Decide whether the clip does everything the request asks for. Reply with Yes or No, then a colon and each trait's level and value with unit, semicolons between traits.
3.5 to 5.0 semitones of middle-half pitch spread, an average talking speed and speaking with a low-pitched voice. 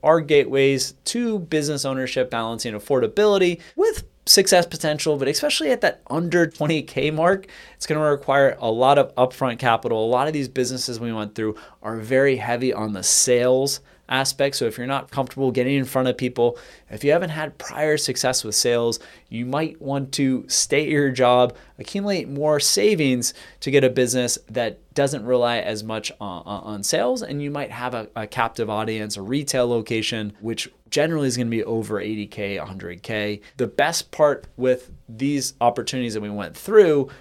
Yes: average, 4.2 semitones; average, 180 wpm; low, 130 Hz